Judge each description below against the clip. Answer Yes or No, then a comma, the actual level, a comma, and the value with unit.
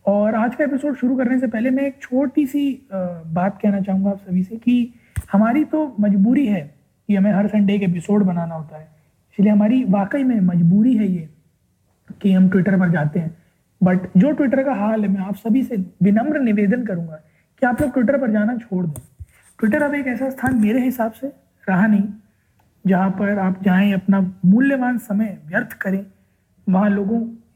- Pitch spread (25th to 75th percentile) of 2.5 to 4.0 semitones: No, average, 4.9 semitones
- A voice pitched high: Yes, high, 205 Hz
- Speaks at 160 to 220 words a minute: Yes, average, 185 wpm